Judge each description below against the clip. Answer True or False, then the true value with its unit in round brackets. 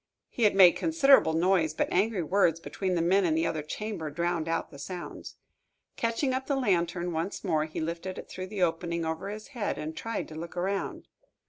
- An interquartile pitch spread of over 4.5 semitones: False (3.6 semitones)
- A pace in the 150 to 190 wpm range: False (205 wpm)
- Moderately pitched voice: True (175 Hz)